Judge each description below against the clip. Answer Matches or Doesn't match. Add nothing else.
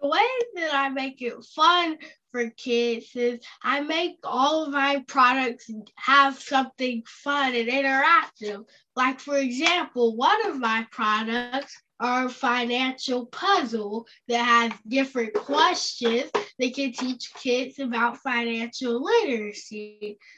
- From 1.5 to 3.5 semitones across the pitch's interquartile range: Matches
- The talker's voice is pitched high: Matches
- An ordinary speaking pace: Doesn't match